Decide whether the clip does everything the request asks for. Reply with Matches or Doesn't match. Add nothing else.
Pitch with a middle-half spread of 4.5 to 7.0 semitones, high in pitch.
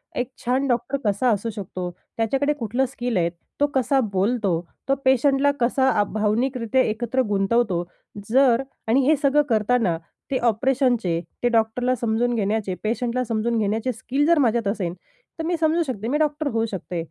Doesn't match